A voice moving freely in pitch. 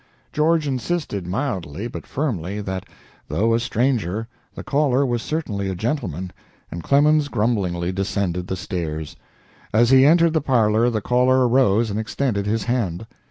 Yes: wide, 5.7 semitones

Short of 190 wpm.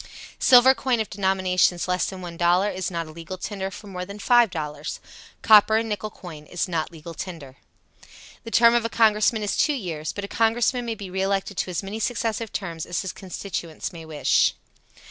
No: average, 195 wpm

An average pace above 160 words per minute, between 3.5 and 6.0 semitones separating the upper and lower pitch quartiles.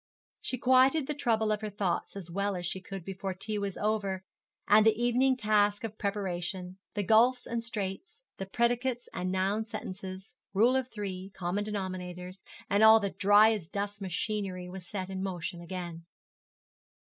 No: average, 170 wpm; average, 2.9 semitones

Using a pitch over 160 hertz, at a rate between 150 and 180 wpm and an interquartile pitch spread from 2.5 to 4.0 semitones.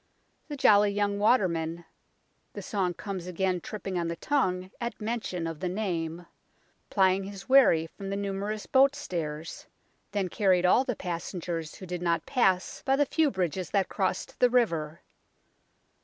Yes: high, 190 Hz; average, 160 wpm; average, 3.5 semitones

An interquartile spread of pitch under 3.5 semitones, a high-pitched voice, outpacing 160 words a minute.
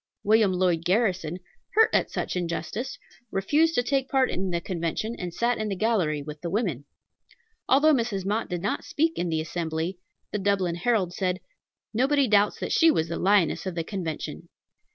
No: average, 5.3 semitones; high, 195 Hz; average, 180 wpm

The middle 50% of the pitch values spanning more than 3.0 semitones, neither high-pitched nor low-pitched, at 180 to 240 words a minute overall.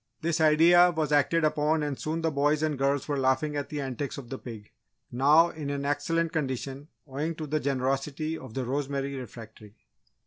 No: narrow, 2.4 semitones; medium, 145 Hz; average, 185 wpm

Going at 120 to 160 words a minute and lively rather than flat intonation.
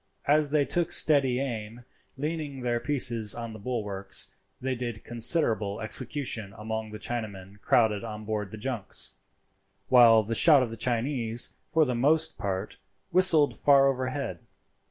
No: average, 145 wpm; average, 4.2 semitones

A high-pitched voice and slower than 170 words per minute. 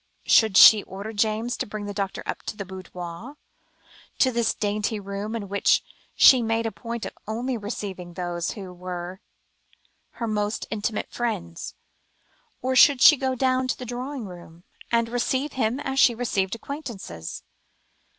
Yes: high, 220 Hz; average, 160 wpm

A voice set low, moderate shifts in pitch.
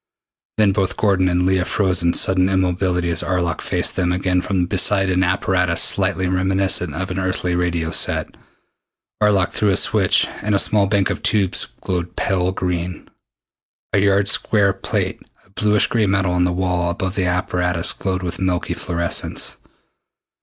No: very low, 95 Hz; narrow, 1.5 semitones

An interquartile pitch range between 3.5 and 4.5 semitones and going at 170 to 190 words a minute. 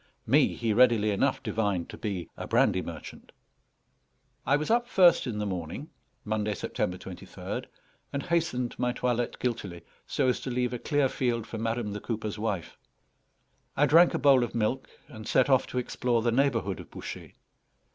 Yes: average, 3.8 semitones; average, 175 wpm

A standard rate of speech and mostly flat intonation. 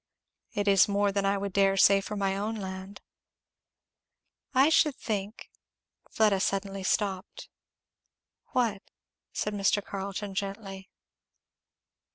No: slow, 125 wpm; narrow, 1.1 semitones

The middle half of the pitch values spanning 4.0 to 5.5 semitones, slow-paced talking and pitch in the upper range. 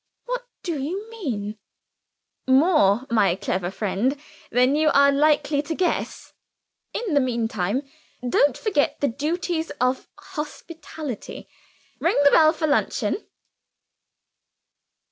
Yes: average, 4.8 semitones; slow, 110 wpm; very high, 285 Hz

